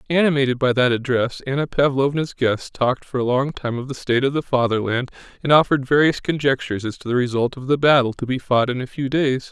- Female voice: No, male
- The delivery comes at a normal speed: No, fast, 225 wpm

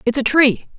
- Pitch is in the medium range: No, very high, 250 Hz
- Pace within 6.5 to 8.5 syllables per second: No, 5.0 syllables/s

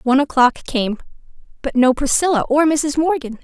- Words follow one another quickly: No, average, 155 wpm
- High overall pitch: Yes, very high, 275 Hz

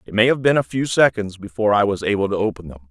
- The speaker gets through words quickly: Yes, fast, 290 wpm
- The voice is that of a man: Yes, male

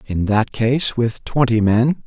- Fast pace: No, average, 175 wpm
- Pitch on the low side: Yes, low, 120 Hz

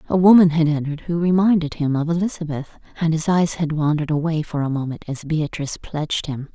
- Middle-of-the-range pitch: Yes, medium, 160 Hz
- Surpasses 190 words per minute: Yes, average, 200 wpm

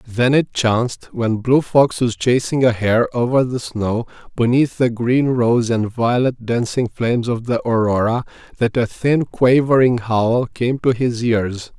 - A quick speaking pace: No, average, 170 wpm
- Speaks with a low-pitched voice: Yes, low, 120 Hz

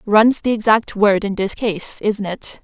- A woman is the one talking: Yes, female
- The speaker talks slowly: No, fast, 205 wpm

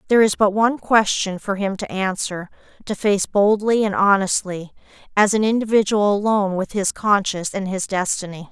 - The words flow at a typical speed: Yes, average, 170 wpm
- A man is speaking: No, female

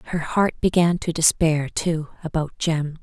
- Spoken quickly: No, average, 160 wpm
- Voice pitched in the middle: Yes, medium, 160 Hz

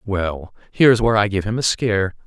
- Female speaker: No, male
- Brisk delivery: Yes, fast, 210 wpm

